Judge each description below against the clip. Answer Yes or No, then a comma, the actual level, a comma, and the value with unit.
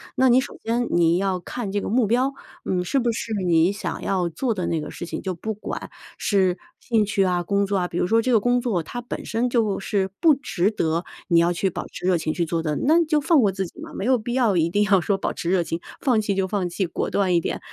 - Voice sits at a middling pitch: No, high, 195 Hz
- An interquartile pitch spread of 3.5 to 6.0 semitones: Yes, average, 5.1 semitones